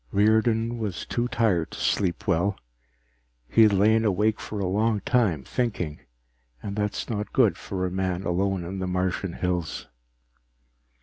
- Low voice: Yes, low, 100 Hz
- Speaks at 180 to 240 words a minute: No, average, 165 wpm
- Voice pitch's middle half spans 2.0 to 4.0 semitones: Yes, average, 3.2 semitones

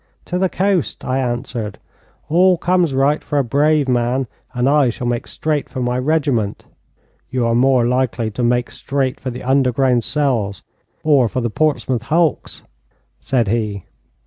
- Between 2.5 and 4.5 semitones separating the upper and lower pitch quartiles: Yes, average, 3.5 semitones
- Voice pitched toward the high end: No, low, 130 Hz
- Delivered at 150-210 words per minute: Yes, average, 160 wpm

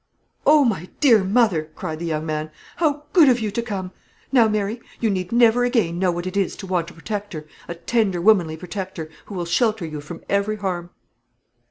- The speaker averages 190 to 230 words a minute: Yes, average, 200 wpm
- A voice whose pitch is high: Yes, high, 195 Hz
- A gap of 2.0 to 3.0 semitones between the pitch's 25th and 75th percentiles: No, average, 4.7 semitones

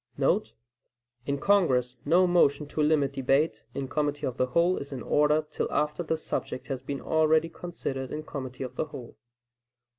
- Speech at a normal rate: Yes, average, 175 wpm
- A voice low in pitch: No, medium, 145 Hz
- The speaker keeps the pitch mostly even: No, average, 3.3 semitones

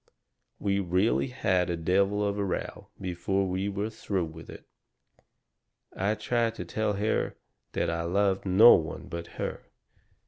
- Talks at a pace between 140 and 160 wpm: Yes, average, 150 wpm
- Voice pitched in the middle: No, low, 100 Hz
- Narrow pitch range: Yes, narrow, 2.3 semitones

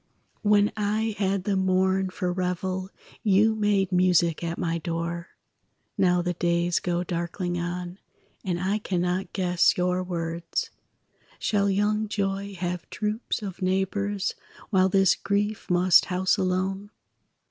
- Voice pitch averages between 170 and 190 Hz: Yes, medium, 185 Hz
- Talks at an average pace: No, slow, 130 wpm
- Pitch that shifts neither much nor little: No, narrow, 2.1 semitones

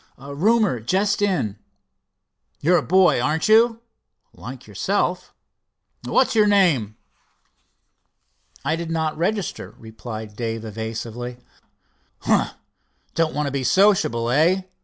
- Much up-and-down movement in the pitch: Yes, wide, 8.6 semitones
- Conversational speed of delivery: No, slow, 110 wpm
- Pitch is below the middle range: No, medium, 155 Hz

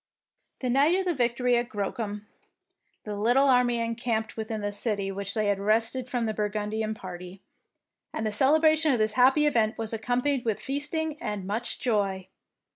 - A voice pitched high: Yes, high, 225 Hz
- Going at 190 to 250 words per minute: No, average, 170 wpm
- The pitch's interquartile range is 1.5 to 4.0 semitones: Yes, average, 3.5 semitones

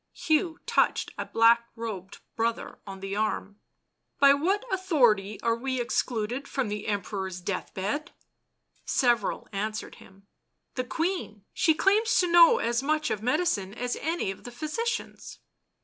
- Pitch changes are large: Yes, wide, 7.0 semitones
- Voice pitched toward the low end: No, high, 235 Hz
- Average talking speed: Yes, average, 155 wpm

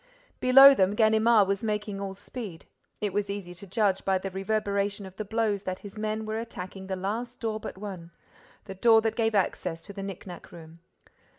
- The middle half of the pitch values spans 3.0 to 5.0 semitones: No, narrow, 2.4 semitones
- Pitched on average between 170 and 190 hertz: No, high, 200 Hz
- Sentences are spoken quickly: No, average, 195 wpm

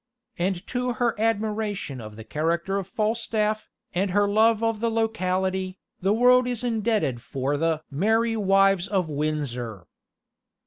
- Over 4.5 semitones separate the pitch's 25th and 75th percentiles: Yes, average, 5.3 semitones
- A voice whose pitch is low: No, high, 195 Hz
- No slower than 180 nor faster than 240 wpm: No, average, 140 wpm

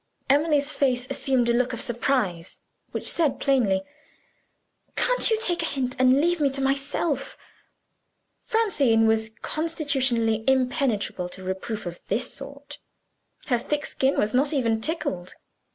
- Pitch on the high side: Yes, very high, 265 Hz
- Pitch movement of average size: Yes, average, 4.4 semitones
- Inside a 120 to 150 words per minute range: Yes, slow, 135 wpm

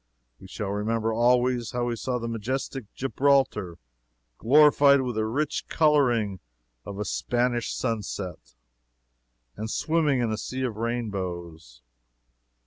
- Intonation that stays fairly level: No, average, 3.8 semitones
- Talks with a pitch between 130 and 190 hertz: No, low, 115 Hz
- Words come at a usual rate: No, slow, 120 wpm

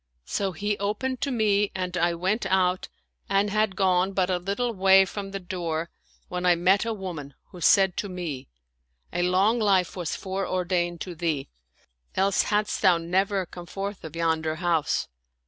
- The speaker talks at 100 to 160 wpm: No, average, 180 wpm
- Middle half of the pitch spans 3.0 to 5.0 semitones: No, narrow, 2.4 semitones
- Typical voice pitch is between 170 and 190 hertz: Yes, medium, 185 Hz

